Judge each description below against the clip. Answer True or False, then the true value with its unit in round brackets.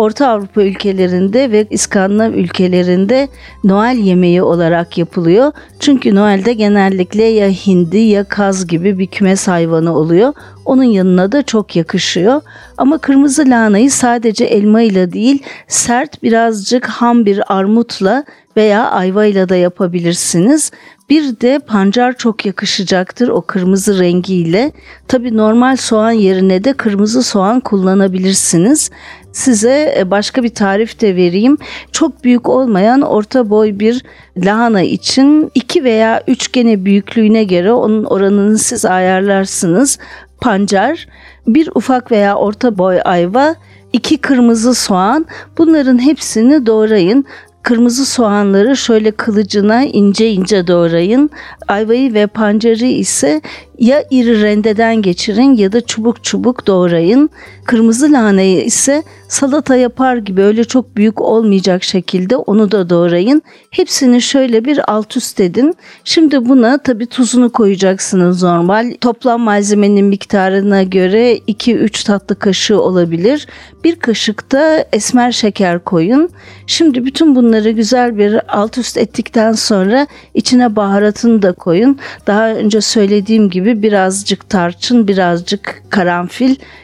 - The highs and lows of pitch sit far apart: False (4.3 semitones)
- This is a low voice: False (220 Hz)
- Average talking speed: True (120 wpm)